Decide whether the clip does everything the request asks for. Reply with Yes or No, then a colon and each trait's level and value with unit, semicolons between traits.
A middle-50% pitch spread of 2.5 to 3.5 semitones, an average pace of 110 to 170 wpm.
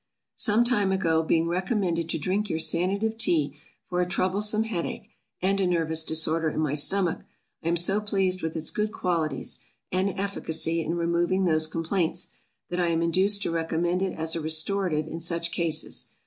No: average, 3.0 semitones; average, 180 wpm